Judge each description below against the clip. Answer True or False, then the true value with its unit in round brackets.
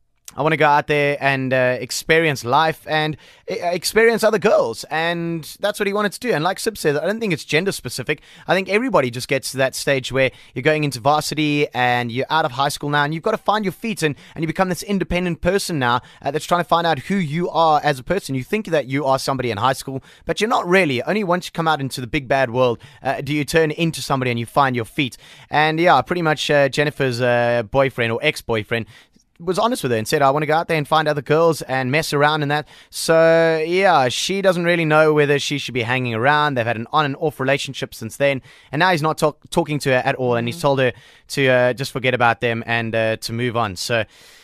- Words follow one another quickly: True (260 wpm)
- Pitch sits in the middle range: True (150 Hz)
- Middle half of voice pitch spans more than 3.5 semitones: True (4.2 semitones)